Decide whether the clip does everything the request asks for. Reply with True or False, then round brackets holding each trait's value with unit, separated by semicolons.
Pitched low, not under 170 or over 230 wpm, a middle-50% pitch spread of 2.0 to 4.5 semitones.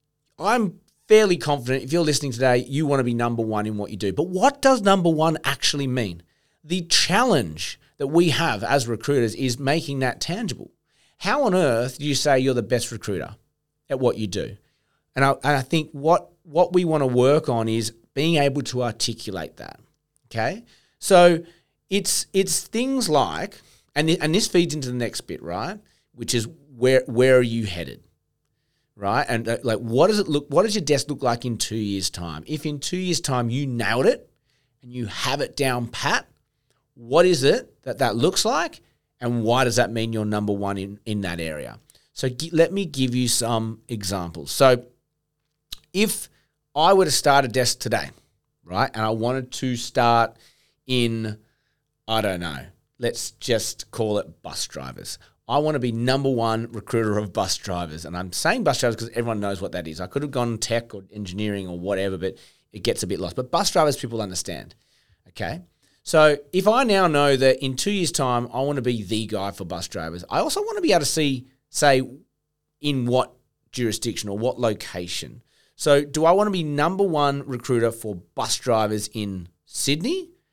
False (130 Hz; 195 wpm; 4.9 semitones)